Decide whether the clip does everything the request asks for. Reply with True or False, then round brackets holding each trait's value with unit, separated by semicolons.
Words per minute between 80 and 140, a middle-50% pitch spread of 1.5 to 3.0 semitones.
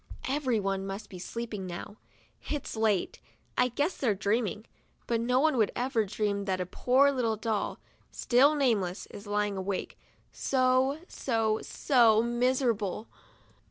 False (135 wpm; 3.9 semitones)